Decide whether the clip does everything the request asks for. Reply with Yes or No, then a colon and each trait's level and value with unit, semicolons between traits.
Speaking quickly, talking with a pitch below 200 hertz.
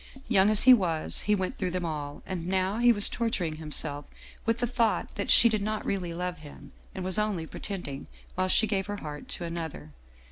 Yes: fast, 210 wpm; medium, 185 Hz